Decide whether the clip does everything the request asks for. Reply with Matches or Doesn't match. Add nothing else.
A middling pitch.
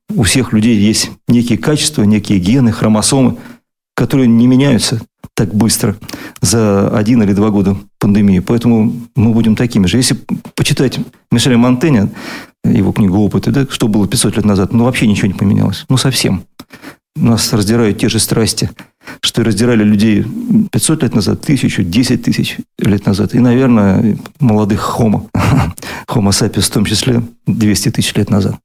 Doesn't match